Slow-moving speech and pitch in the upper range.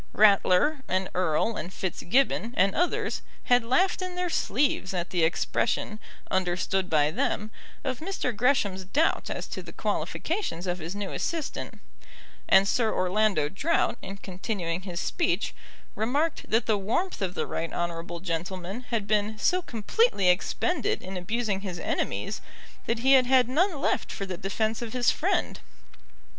No: average, 155 wpm; high, 210 Hz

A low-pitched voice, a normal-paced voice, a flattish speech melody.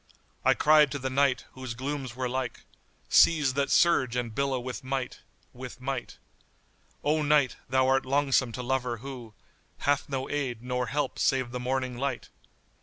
Yes: low, 130 Hz; average, 175 wpm; narrow, 1.7 semitones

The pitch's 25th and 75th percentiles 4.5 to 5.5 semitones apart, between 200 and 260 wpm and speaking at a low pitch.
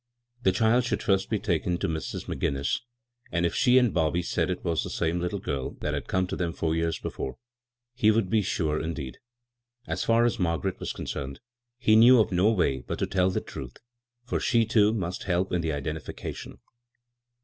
Yes: average, 5.2 semitones; fast, 205 wpm; very low, 90 Hz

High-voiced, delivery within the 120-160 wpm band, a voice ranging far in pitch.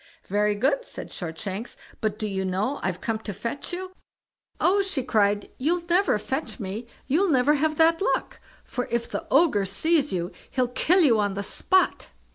No: high, 245 Hz; average, 180 wpm; wide, 7.9 semitones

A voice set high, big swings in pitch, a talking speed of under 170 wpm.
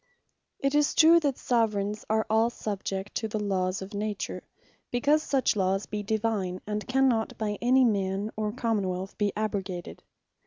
No: high, 215 Hz; average, 3.2 semitones; average, 160 wpm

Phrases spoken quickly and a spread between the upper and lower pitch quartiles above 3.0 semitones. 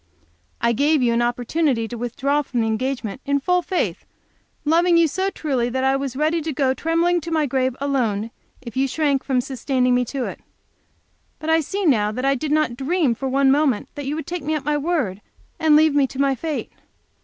Yes: fast, 215 wpm; average, 3.8 semitones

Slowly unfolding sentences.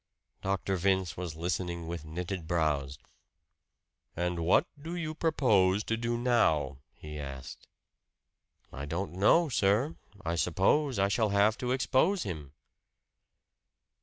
Yes: slow, 125 wpm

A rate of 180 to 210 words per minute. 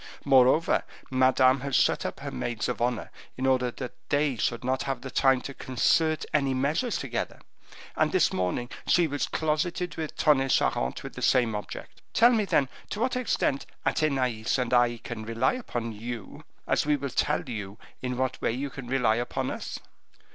Yes: average, 185 wpm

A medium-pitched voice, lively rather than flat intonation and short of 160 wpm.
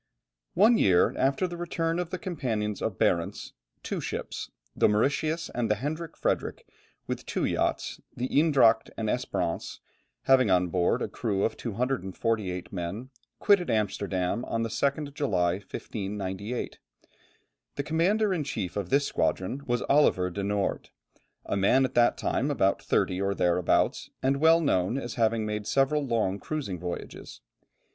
No: low, 115 Hz; wide, 6.5 semitones; average, 150 wpm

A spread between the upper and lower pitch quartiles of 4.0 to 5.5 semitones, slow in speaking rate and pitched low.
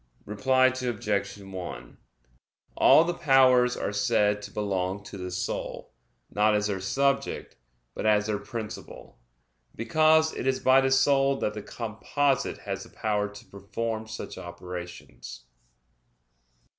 Yes: average, 4.5 semitones; slow, 130 wpm; low, 110 Hz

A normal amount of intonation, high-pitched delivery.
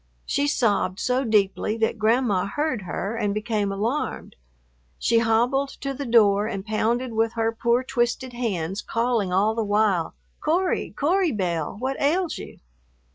Yes: average, 3.8 semitones; high, 225 Hz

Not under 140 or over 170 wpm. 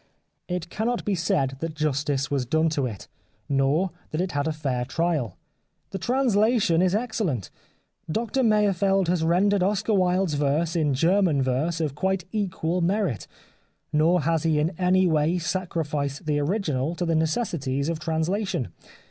Yes: average, 155 wpm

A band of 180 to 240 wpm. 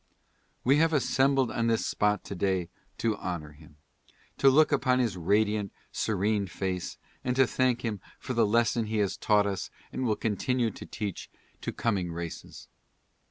No: average, 170 wpm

